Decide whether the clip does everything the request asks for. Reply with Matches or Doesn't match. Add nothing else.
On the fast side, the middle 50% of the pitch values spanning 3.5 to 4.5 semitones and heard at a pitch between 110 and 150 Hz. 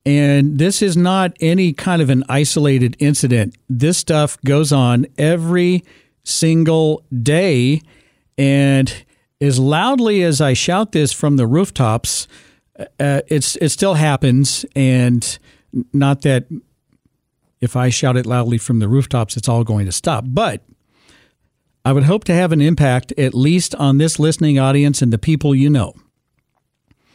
Doesn't match